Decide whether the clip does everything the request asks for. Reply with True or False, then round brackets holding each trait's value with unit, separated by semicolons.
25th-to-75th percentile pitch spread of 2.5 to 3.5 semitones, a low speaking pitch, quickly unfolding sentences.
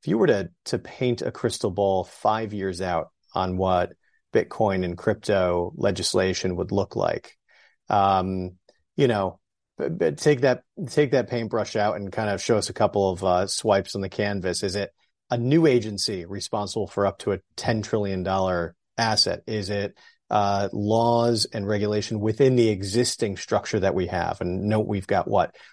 False (2.9 semitones; 100 Hz; 180 wpm)